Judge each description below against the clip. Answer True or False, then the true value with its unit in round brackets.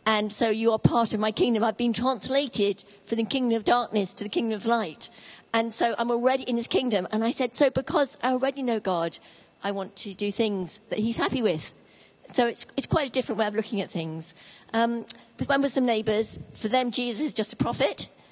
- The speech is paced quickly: True (240 wpm)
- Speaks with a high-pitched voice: True (230 Hz)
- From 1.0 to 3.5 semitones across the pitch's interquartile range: True (3.0 semitones)